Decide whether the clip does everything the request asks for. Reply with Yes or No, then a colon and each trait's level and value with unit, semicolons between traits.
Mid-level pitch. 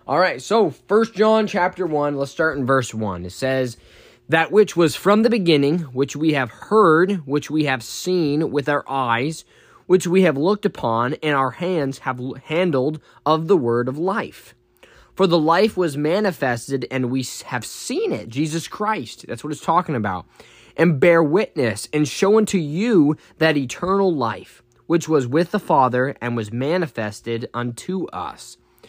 Yes: medium, 150 Hz